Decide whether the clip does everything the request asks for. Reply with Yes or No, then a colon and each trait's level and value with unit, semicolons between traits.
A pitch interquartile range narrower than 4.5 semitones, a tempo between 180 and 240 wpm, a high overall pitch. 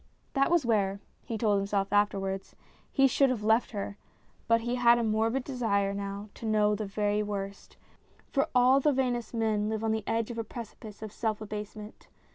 Yes: narrow, 2.5 semitones; average, 195 wpm; high, 220 Hz